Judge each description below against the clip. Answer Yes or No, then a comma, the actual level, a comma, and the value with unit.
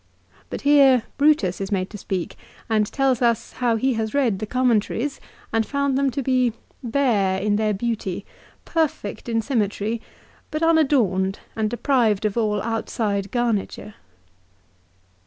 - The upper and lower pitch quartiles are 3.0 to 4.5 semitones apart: Yes, average, 4.1 semitones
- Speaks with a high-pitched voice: Yes, high, 225 Hz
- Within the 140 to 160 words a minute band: Yes, average, 150 wpm